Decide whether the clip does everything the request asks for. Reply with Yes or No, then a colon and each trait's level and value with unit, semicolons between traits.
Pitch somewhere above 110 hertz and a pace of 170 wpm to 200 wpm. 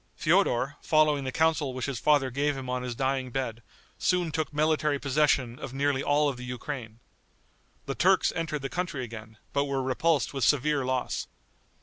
Yes: medium, 140 Hz; average, 180 wpm